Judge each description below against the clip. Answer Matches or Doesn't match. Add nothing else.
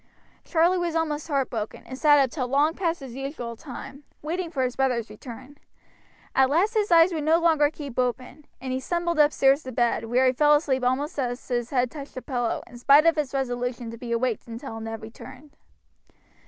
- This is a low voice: Doesn't match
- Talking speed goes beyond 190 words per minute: Matches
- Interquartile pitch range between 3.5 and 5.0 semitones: Matches